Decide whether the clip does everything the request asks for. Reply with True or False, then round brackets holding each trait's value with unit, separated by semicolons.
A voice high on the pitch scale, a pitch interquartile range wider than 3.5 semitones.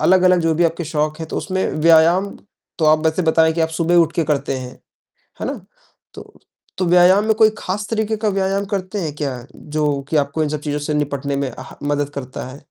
False (160 Hz; 4.0 semitones)